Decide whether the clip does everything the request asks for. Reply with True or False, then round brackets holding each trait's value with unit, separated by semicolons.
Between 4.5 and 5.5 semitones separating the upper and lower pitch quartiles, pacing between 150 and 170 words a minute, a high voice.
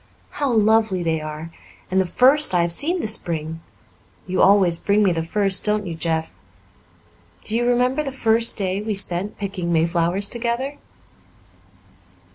True (5.1 semitones; 155 wpm; 200 Hz)